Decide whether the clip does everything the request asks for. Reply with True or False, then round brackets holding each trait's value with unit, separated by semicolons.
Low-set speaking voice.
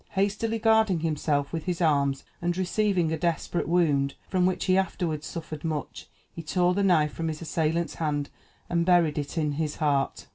False (165 Hz)